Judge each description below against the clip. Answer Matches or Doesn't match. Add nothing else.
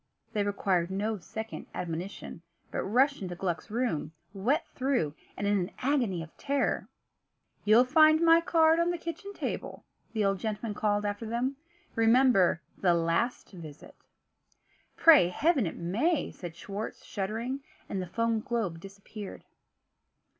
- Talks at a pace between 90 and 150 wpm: Matches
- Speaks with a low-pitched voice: Doesn't match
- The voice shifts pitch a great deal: Matches